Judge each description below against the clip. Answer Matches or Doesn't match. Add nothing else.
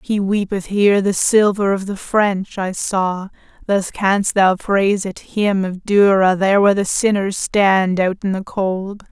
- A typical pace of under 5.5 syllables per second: Matches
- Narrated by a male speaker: Doesn't match